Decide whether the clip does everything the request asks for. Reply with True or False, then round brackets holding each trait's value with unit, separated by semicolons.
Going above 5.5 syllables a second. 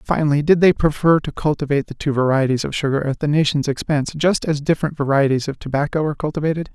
True (6.8 syllables/s)